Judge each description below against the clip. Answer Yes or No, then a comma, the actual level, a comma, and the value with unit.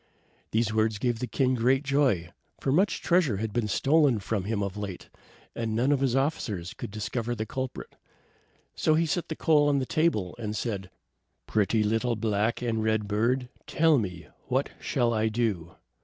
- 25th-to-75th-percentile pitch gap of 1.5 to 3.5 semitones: No, average, 4.2 semitones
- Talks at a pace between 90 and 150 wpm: No, average, 180 wpm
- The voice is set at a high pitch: No, low, 115 Hz